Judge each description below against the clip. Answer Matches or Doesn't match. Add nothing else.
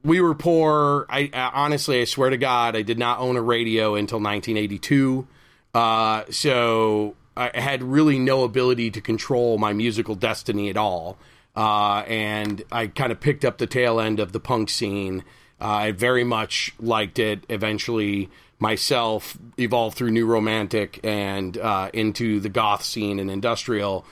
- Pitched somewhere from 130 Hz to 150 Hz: Doesn't match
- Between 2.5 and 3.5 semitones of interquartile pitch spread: Matches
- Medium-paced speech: Matches